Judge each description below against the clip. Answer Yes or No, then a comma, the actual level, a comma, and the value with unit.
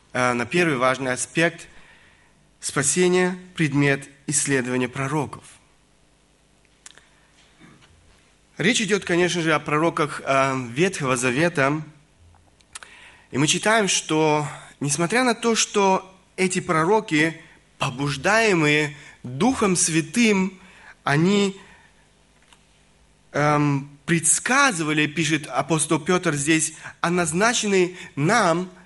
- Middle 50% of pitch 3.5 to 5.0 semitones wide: Yes, average, 4.5 semitones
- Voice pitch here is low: No, medium, 160 Hz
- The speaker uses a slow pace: Yes, slow, 80 wpm